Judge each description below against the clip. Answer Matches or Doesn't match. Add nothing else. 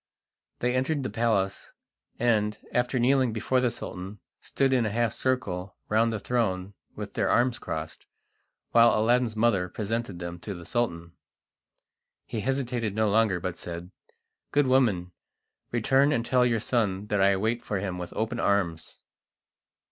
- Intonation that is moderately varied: Matches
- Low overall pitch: Matches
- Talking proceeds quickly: Doesn't match